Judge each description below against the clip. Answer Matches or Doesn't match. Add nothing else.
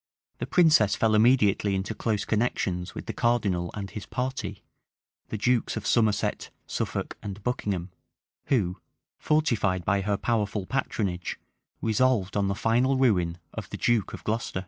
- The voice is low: Matches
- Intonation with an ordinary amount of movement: Matches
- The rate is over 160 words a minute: Doesn't match